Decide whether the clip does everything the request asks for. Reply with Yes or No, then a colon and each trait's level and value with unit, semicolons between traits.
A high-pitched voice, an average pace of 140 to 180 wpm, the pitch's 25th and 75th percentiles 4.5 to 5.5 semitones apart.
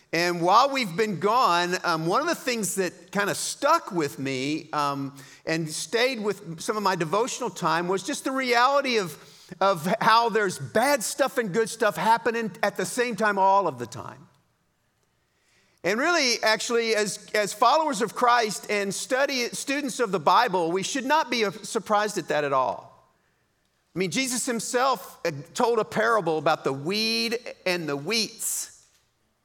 Yes: high, 210 Hz; average, 170 wpm; average, 5.1 semitones